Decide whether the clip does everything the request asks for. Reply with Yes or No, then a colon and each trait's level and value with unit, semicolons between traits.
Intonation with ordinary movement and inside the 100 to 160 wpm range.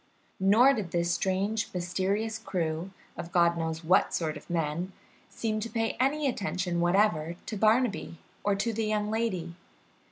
Yes: average, 4.2 semitones; average, 155 wpm